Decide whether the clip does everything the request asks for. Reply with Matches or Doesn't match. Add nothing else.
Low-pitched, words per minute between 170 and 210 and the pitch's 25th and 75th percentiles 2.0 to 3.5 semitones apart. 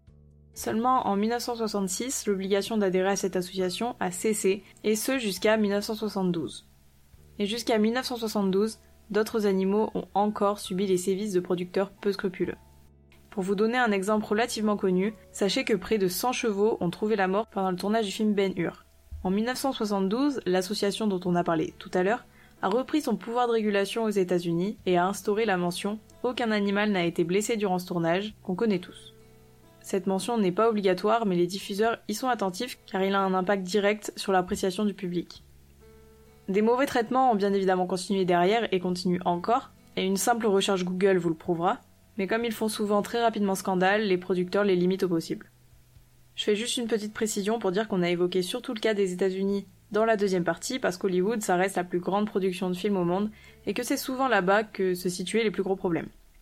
Doesn't match